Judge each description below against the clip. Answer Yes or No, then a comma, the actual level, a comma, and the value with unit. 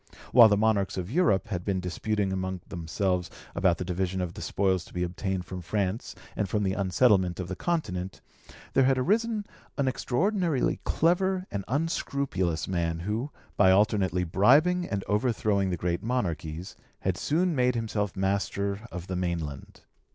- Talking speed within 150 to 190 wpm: Yes, average, 160 wpm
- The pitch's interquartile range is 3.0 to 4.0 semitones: No, wide, 5.5 semitones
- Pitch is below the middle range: Yes, low, 100 Hz